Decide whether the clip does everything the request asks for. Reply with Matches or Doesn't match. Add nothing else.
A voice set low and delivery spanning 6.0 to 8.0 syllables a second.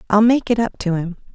Doesn't match